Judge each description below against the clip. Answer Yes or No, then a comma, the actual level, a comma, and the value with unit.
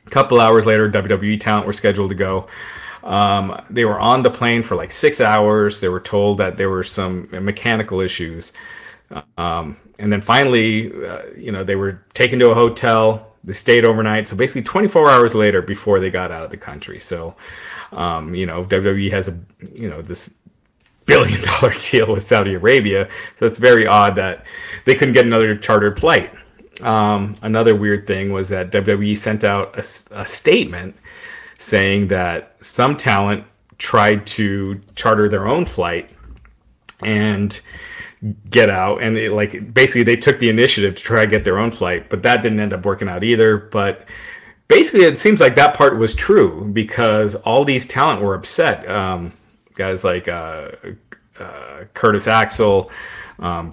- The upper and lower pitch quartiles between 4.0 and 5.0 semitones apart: No, narrow, 2.5 semitones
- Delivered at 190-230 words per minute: No, average, 175 wpm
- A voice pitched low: Yes, low, 105 Hz